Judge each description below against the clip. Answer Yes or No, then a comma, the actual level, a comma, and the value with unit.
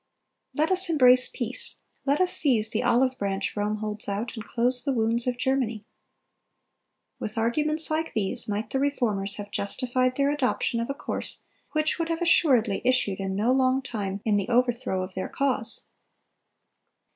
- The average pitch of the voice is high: Yes, high, 245 Hz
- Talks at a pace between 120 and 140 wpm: No, average, 170 wpm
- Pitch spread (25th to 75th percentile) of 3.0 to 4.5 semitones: Yes, average, 4.2 semitones